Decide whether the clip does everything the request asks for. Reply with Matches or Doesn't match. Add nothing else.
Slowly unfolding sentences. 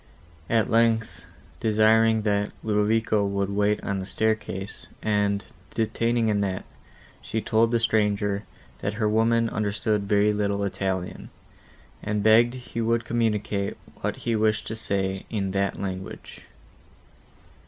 Matches